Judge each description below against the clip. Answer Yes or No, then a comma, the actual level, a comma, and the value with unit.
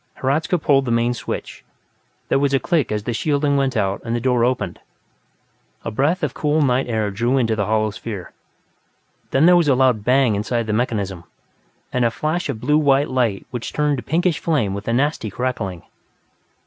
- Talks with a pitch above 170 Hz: No, low, 125 Hz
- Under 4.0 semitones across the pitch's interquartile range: No, average, 4.4 semitones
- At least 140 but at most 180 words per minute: No, average, 195 wpm